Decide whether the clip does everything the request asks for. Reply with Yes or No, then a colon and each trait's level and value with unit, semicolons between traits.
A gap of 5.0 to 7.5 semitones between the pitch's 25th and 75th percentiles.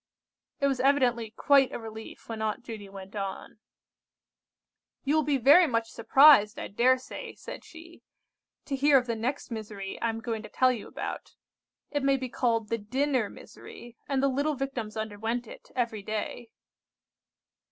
No: average, 3.9 semitones